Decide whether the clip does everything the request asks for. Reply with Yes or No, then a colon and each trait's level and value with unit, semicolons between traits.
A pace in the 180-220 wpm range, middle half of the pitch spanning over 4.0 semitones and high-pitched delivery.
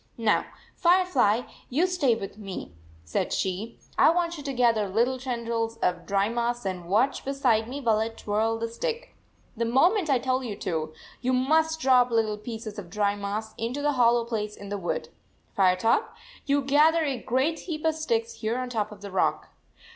Yes: average, 190 wpm; average, 4.8 semitones; high, 235 Hz